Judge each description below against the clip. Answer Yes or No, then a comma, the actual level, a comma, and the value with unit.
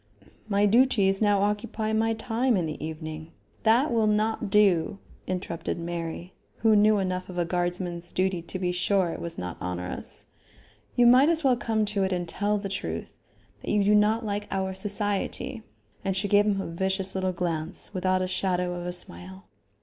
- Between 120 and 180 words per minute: No, average, 190 wpm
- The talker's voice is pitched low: No, high, 195 Hz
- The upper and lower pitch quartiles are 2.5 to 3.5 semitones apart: Yes, average, 3.1 semitones